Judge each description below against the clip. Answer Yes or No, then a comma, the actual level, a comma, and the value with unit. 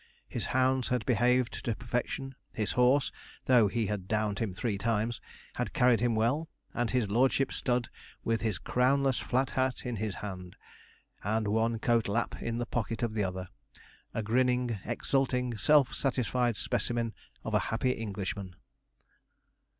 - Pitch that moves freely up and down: No, narrow, 2.6 semitones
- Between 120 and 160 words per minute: Yes, average, 155 wpm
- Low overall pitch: Yes, low, 115 Hz